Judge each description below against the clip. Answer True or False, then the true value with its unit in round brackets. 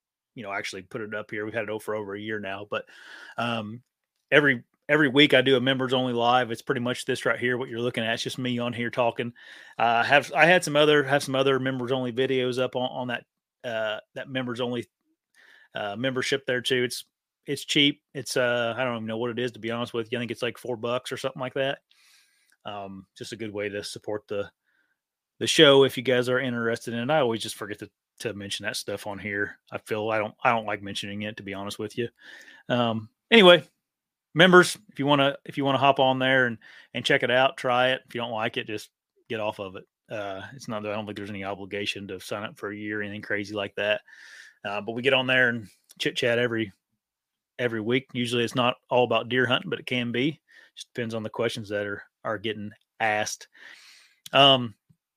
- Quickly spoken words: True (240 wpm)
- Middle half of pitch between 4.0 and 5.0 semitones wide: False (3.3 semitones)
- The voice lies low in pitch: True (120 Hz)